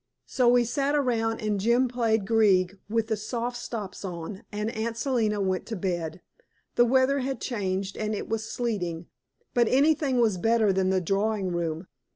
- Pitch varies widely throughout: No, average, 3.9 semitones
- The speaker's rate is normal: Yes, average, 175 wpm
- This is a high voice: Yes, high, 220 Hz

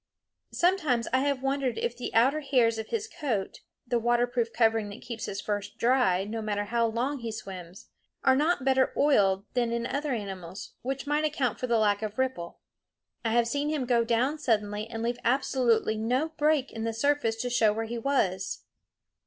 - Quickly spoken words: No, average, 190 wpm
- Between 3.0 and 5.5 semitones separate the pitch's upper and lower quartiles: Yes, average, 3.4 semitones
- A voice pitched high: Yes, high, 235 Hz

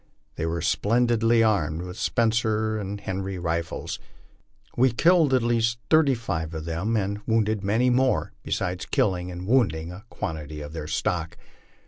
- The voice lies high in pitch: No, low, 100 Hz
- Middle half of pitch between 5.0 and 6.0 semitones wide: Yes, wide, 5.5 semitones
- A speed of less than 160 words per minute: Yes, average, 150 wpm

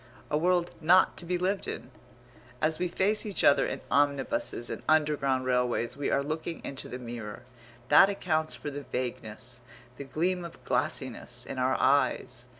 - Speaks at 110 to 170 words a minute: Yes, average, 165 wpm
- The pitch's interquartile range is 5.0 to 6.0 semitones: Yes, wide, 5.4 semitones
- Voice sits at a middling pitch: Yes, medium, 150 Hz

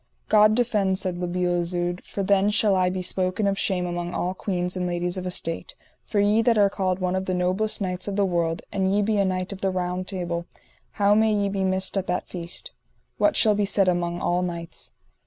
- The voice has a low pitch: No, medium, 185 Hz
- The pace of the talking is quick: Yes, fast, 225 wpm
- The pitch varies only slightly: Yes, narrow, 2.1 semitones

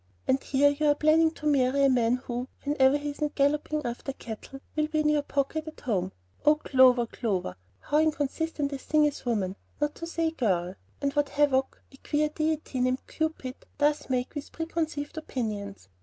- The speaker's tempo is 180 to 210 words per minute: Yes, average, 185 wpm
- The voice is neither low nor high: No, very high, 285 Hz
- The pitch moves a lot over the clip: No, average, 3.1 semitones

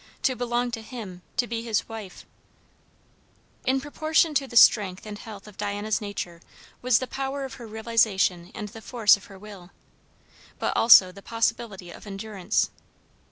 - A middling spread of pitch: Yes, average, 3.2 semitones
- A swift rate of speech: No, average, 160 wpm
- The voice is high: Yes, high, 220 Hz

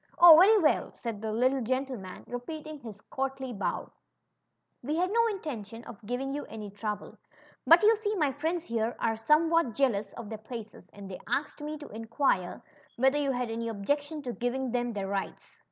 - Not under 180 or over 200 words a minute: Yes, average, 190 wpm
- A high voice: Yes, very high, 255 Hz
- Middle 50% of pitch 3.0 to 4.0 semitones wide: No, average, 5.2 semitones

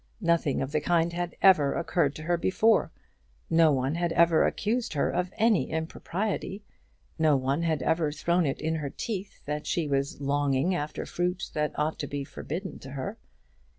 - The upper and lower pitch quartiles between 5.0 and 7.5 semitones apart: No, average, 3.5 semitones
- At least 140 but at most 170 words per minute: No, average, 180 wpm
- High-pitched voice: No, medium, 160 Hz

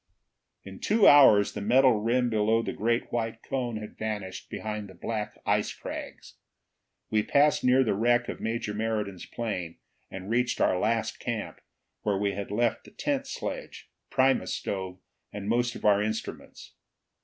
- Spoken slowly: No, average, 160 wpm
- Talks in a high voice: No, low, 110 Hz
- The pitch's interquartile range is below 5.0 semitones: Yes, average, 2.8 semitones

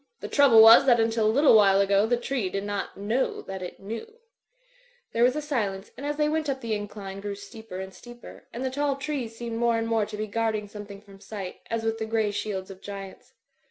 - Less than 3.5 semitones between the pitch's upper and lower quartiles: Yes, average, 3.1 semitones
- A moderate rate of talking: No, fast, 235 wpm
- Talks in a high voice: Yes, high, 220 Hz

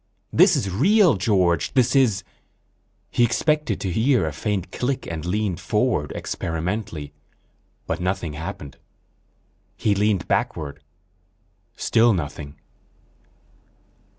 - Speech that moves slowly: Yes, slow, 105 wpm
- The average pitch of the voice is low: Yes, low, 100 Hz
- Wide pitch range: Yes, wide, 6.2 semitones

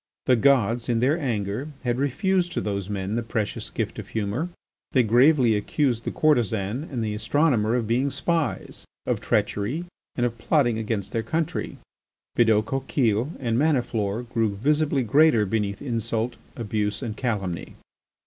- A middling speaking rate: Yes, average, 150 wpm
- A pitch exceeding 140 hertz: No, low, 120 Hz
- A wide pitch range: No, average, 4.5 semitones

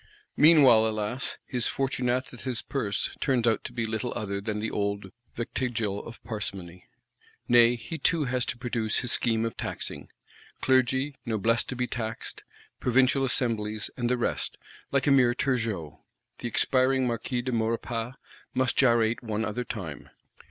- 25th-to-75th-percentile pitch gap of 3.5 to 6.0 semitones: No, narrow, 2.6 semitones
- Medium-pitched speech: No, low, 120 Hz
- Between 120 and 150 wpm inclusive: Yes, average, 145 wpm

